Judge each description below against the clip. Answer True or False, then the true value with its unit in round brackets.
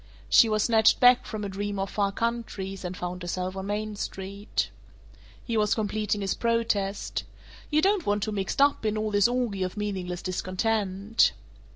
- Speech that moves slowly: False (180 wpm)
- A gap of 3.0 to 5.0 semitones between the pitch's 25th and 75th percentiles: False (2.6 semitones)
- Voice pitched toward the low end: False (205 Hz)